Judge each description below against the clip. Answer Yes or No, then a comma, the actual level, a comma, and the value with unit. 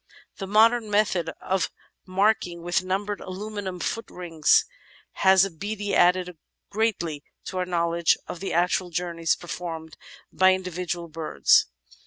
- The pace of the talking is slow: Yes, slow, 125 wpm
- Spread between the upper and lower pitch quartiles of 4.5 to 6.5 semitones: No, narrow, 2.6 semitones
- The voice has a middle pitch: Yes, medium, 180 Hz